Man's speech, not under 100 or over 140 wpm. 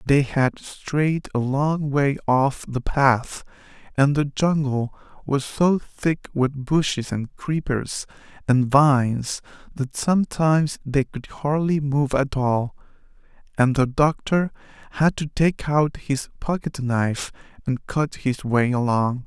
Yes: male; slow, 135 wpm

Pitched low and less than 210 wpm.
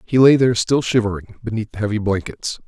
Yes: low, 110 Hz; average, 200 wpm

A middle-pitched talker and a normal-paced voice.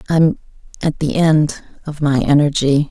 Yes: medium, 150 Hz; average, 145 wpm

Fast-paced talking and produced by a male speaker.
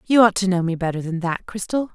No: fast, 280 wpm; female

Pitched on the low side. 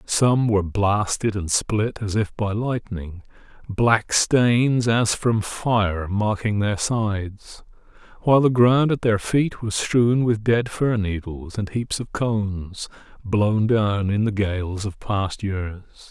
Yes: low, 105 Hz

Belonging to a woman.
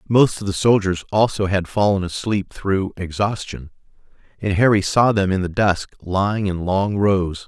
No: male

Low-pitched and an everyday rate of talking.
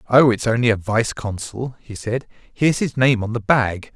No: low, 115 Hz; fast, 210 wpm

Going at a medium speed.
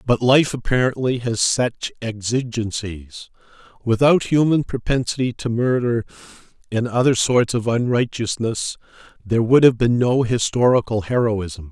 No: slow, 120 wpm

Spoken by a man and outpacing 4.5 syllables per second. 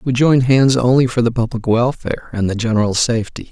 Yes: male; 6.1 syllables/s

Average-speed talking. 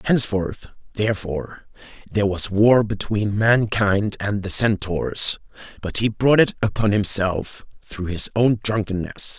No: slow, 130 wpm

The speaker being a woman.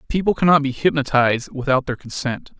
No: male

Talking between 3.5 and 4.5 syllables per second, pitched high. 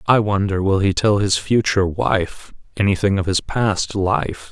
No: 4.3 syllables/s; low, 100 Hz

